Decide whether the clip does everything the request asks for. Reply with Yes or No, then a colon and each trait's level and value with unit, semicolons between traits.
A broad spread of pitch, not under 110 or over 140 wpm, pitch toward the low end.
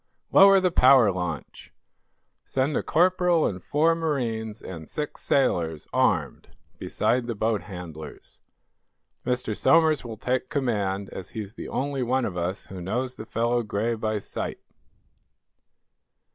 Yes: wide, 5.7 semitones; slow, 135 wpm; low, 115 Hz